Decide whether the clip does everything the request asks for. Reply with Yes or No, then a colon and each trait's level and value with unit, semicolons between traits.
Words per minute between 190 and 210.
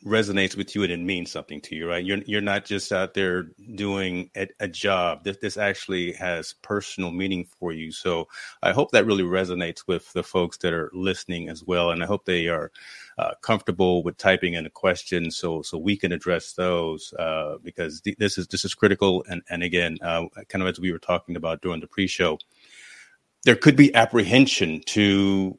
Yes: fast, 205 wpm